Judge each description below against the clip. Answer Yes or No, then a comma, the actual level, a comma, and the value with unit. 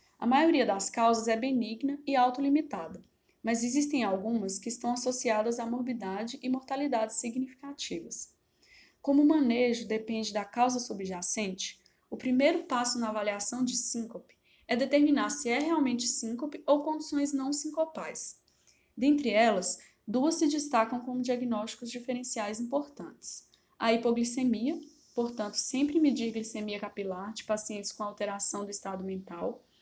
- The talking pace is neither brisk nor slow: Yes, average, 135 wpm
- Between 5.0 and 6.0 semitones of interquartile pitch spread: No, average, 4.3 semitones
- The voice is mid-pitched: No, high, 240 Hz